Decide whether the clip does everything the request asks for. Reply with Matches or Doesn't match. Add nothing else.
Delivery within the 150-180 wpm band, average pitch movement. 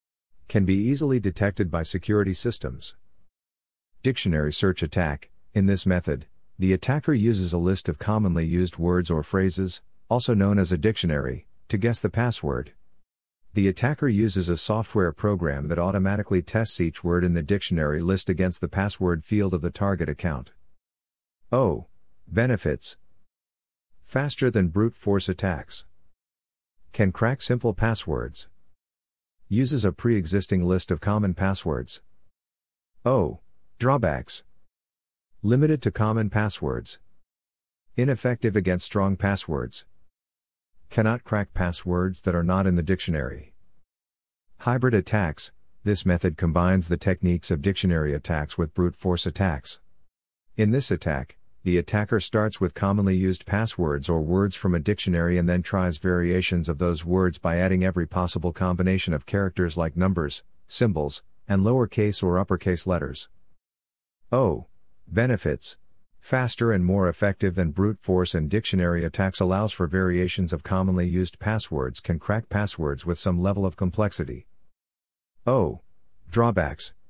Doesn't match